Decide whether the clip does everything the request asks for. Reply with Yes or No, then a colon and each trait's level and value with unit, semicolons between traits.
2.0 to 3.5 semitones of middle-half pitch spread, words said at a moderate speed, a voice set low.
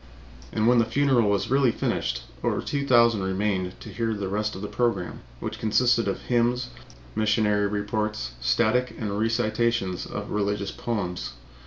Yes: average, 2.8 semitones; average, 155 wpm; low, 110 Hz